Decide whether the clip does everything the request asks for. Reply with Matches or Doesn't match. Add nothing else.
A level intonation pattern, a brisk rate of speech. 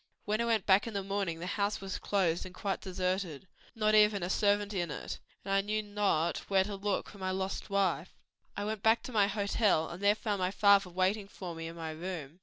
Matches